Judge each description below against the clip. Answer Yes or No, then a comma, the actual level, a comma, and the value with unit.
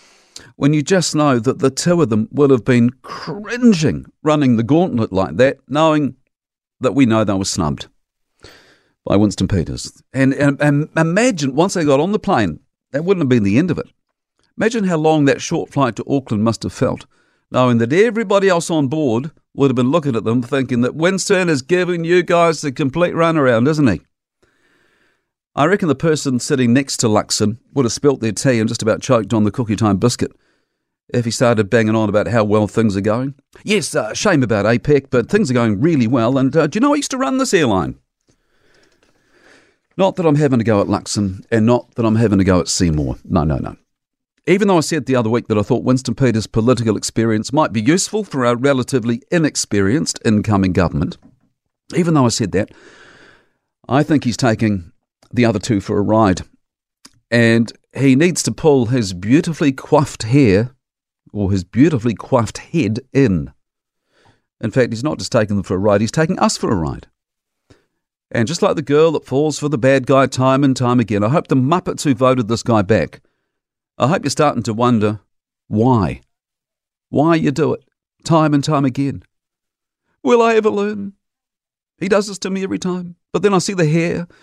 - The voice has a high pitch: No, low, 130 Hz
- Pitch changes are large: Yes, wide, 5.8 semitones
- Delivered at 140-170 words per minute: No, average, 200 wpm